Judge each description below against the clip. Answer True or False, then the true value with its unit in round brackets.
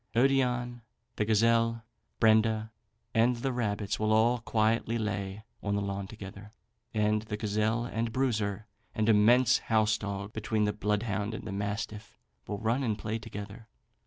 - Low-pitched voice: True (110 Hz)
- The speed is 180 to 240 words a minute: False (145 wpm)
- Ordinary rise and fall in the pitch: False (1.8 semitones)